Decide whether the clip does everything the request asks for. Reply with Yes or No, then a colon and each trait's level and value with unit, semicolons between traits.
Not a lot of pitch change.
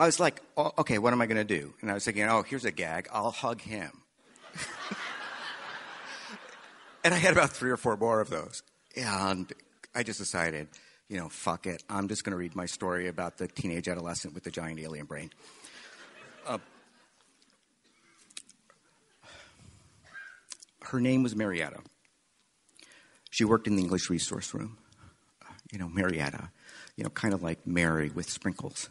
No: average, 4.4 semitones